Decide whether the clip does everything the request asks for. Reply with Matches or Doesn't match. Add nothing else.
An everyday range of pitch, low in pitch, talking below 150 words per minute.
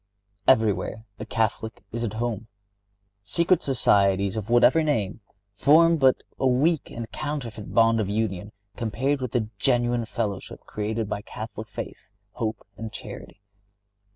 Matches